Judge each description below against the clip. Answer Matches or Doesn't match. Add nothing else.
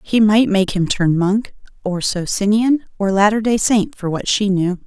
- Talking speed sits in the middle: Matches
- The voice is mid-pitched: Doesn't match